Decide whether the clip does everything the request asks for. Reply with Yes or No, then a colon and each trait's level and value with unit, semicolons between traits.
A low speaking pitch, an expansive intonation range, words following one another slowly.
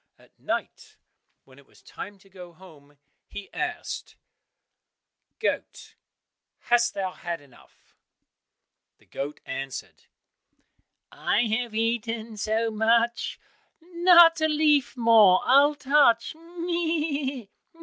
No: high, 235 Hz; wide, 7.2 semitones; slow, 105 wpm